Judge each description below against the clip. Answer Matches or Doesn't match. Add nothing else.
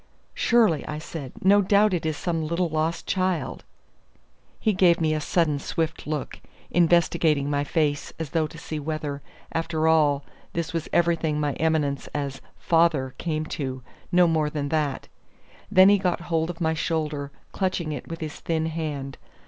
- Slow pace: Doesn't match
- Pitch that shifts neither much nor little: Doesn't match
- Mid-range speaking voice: Matches